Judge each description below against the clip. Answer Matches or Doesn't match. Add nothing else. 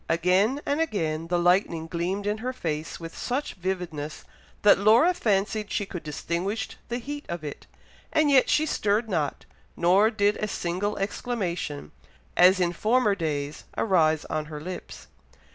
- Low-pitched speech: Doesn't match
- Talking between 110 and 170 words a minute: Matches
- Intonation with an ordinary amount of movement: Matches